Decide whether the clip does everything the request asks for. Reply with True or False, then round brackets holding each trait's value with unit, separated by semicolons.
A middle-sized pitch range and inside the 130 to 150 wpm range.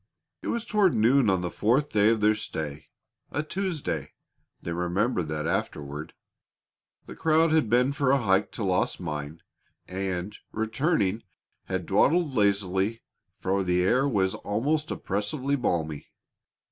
False (7.2 semitones; 140 wpm)